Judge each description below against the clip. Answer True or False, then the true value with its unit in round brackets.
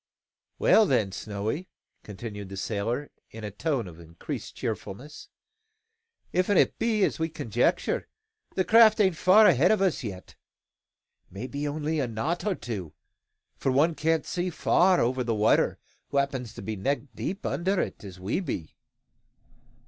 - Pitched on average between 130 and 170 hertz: True (135 Hz)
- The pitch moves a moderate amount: False (8.8 semitones)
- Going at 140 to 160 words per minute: True (150 wpm)